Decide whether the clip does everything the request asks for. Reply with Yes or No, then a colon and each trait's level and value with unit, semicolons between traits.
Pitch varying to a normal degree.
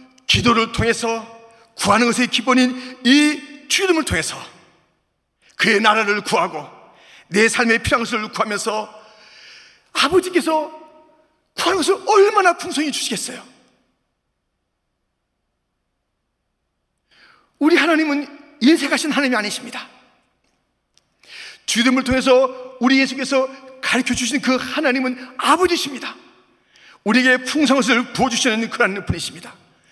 Yes: average, 4.0 semitones